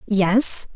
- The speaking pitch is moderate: No, high, 205 Hz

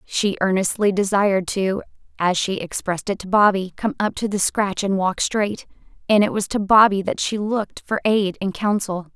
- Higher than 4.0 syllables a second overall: Yes, 5.0 syllables/s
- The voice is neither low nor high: No, high, 200 Hz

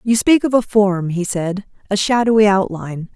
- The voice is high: Yes, high, 205 Hz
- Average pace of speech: Yes, average, 190 wpm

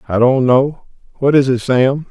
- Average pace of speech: Yes, average, 170 wpm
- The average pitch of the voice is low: Yes, low, 130 Hz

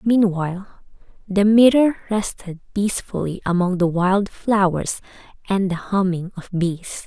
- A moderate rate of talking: No, slow, 120 wpm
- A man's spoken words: No, female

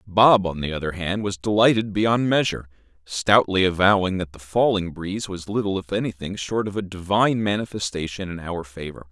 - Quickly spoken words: No, average, 180 wpm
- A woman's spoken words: No, male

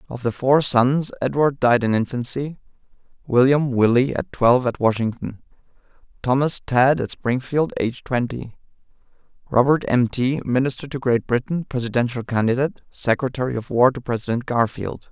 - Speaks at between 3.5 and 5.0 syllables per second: No, 5.4 syllables/s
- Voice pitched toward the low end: Yes, low, 125 Hz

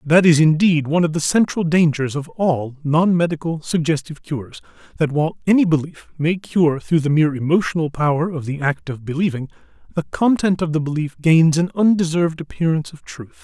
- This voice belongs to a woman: No, male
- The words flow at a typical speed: Yes, average, 185 wpm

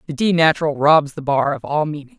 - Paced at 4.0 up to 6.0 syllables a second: Yes, 5.9 syllables/s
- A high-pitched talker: No, medium, 150 Hz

